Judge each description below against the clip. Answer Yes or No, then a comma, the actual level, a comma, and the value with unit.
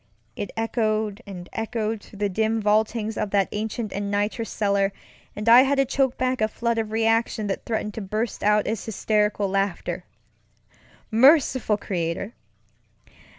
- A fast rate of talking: No, average, 150 wpm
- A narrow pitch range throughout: Yes, narrow, 1.8 semitones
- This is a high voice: Yes, high, 215 Hz